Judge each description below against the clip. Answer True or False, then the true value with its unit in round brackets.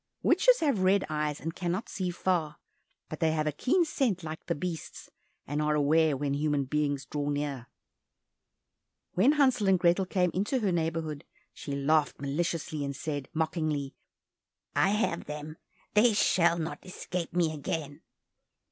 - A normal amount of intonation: True (3.7 semitones)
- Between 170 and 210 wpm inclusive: False (155 wpm)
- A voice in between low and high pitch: True (160 Hz)